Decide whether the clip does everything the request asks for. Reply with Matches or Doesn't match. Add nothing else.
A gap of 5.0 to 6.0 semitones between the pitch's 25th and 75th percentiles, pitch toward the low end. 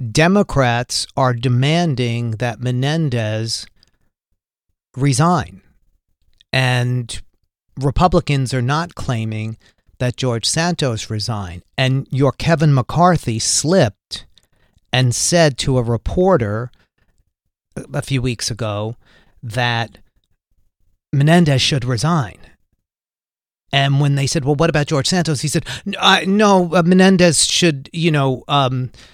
Matches